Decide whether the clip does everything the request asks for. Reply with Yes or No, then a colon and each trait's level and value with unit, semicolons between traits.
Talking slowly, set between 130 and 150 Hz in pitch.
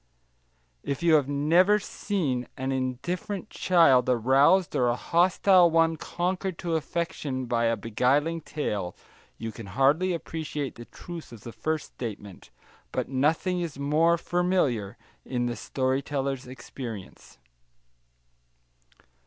Yes: slow, 125 wpm; medium, 140 Hz